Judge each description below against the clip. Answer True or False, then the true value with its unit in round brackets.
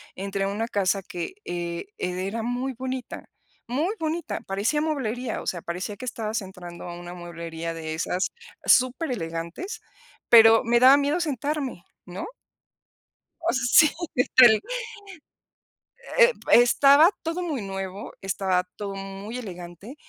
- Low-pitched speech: False (215 Hz)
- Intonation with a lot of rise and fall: True (6.3 semitones)